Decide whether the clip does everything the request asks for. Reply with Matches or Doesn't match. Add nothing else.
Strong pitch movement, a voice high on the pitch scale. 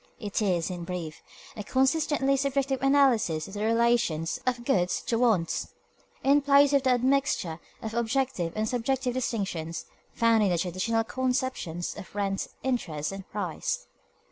Matches